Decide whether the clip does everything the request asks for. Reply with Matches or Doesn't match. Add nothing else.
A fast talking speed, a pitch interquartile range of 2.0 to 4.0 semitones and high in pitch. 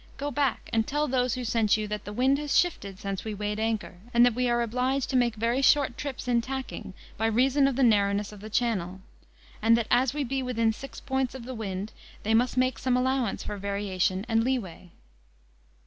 Matches